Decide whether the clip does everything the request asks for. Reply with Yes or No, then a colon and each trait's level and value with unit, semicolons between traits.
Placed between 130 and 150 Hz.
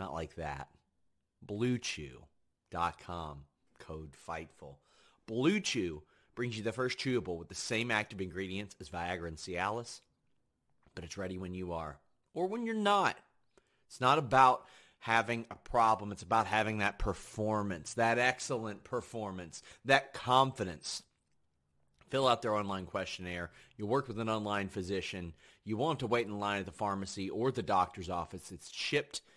No: low, 100 Hz